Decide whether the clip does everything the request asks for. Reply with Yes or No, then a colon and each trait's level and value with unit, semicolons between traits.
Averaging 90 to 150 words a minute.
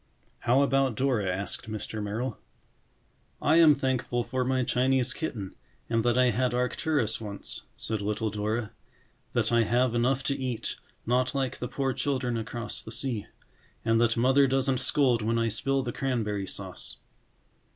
No: average, 160 wpm